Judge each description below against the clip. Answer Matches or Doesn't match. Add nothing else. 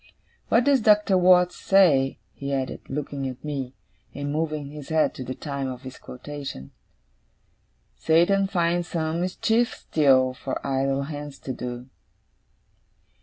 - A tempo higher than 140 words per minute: Doesn't match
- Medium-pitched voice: Matches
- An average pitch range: Matches